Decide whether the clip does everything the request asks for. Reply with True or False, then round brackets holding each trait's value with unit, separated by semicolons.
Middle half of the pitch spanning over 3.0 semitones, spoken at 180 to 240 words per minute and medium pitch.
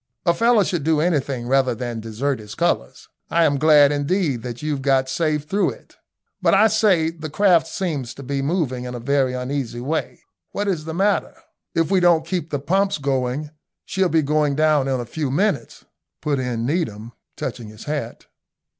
True (4.7 semitones; 190 wpm; 145 Hz)